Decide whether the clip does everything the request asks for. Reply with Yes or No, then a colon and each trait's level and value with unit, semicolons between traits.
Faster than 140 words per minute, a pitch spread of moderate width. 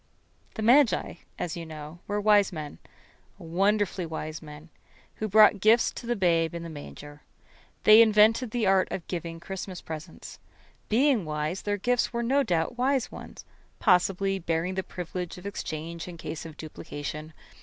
Yes: average, 160 wpm; average, 4.8 semitones